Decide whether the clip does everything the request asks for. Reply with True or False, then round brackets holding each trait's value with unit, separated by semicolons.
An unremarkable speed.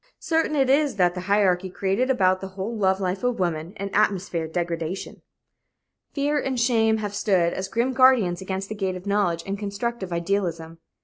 True (185 wpm)